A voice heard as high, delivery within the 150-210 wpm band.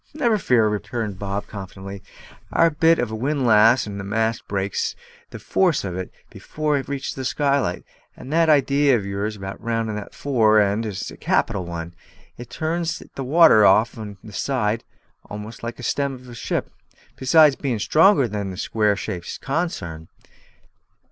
No: low, 115 Hz; average, 175 wpm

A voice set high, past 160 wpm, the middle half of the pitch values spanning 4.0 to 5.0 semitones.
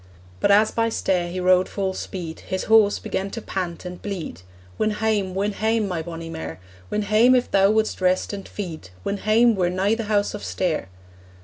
No: high, 195 Hz; average, 200 wpm; average, 2.9 semitones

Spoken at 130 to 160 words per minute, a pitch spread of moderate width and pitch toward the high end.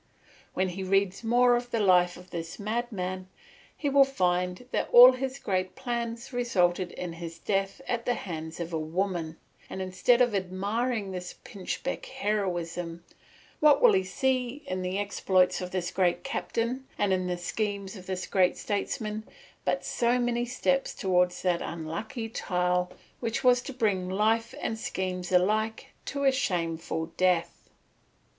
Yes: average, 155 wpm; average, 4.8 semitones; high, 195 Hz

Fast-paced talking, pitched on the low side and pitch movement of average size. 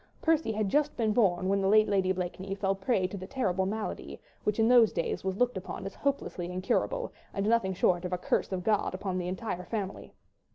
No: fast, 220 wpm; high, 195 Hz; average, 3.1 semitones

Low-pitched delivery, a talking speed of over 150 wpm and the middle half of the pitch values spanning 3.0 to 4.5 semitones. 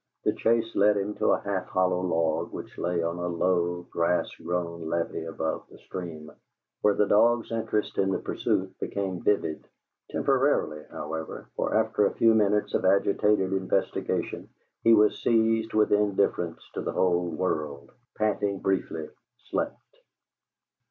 No: very low, 95 Hz; average, 145 wpm; average, 3.6 semitones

